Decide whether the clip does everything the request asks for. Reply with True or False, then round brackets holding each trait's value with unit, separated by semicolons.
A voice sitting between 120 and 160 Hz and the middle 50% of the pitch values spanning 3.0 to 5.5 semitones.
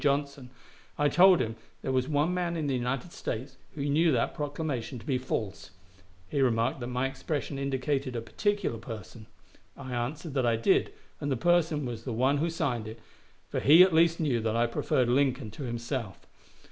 True (135 Hz; 3.8 semitones)